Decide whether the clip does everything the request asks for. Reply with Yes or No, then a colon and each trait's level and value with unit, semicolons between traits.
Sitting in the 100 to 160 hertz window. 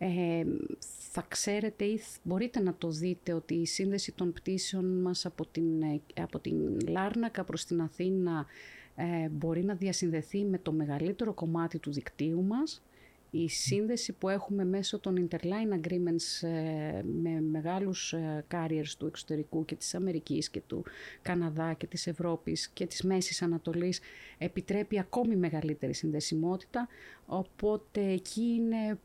No: medium, 175 Hz